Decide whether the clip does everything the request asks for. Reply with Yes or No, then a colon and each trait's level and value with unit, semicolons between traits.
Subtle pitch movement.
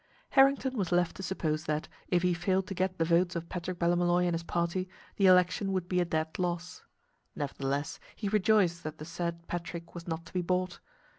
Yes: narrow, 1.6 semitones